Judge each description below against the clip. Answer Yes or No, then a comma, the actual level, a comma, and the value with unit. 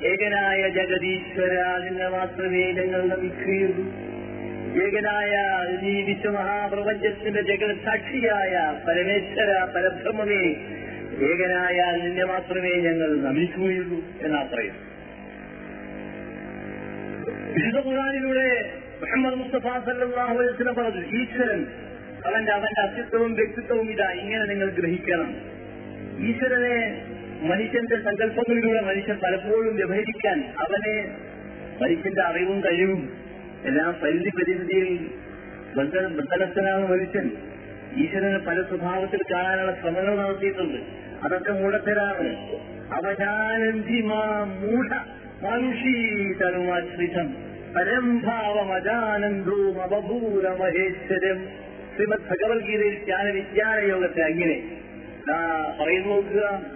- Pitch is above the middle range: Yes, high, 195 Hz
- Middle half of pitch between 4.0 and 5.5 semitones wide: No, average, 3.0 semitones